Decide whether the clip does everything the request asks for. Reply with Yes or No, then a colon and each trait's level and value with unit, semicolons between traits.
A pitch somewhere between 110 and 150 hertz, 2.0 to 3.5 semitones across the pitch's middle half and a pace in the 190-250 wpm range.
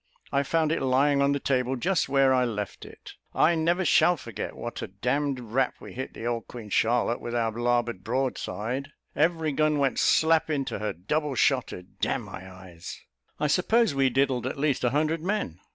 No: low, 135 Hz; average, 4.2 semitones; average, 200 wpm